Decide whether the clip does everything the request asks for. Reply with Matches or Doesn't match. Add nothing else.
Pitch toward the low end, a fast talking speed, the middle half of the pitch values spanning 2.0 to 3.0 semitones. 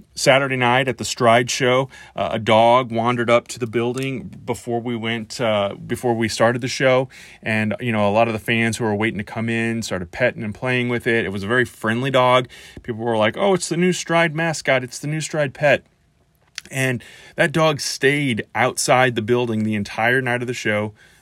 Matches